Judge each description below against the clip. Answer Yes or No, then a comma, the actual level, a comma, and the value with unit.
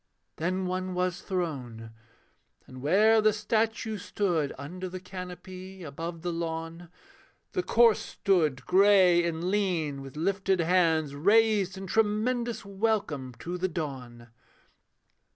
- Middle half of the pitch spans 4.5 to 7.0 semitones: No, average, 3.8 semitones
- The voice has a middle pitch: Yes, medium, 180 Hz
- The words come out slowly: Yes, slow, 120 wpm